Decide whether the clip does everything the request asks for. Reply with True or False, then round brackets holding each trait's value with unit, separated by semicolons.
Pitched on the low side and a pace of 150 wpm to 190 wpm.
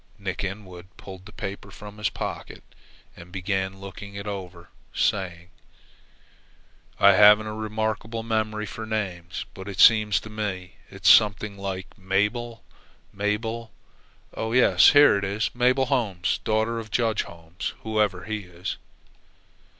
False (105 Hz; 135 wpm)